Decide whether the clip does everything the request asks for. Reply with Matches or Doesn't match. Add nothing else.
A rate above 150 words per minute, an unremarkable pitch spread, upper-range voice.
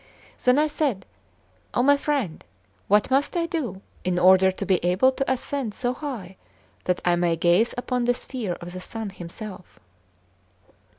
Doesn't match